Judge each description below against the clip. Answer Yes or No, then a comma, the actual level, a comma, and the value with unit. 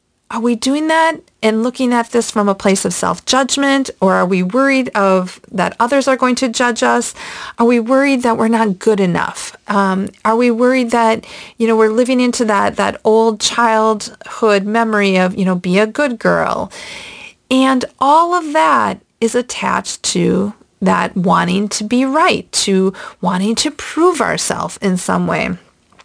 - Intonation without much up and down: No, average, 4.2 semitones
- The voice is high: Yes, high, 230 Hz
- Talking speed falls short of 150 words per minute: No, average, 175 wpm